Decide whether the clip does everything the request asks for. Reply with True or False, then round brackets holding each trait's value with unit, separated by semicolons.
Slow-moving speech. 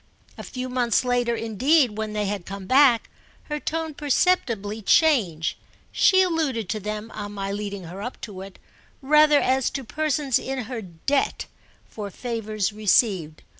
False (155 wpm)